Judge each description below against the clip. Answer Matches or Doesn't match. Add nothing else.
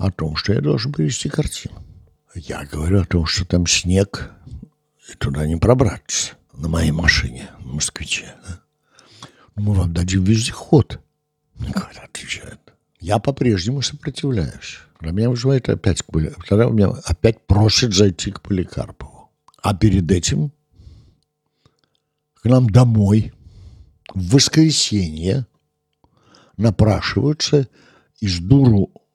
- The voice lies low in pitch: Matches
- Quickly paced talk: Doesn't match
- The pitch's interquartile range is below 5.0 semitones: Doesn't match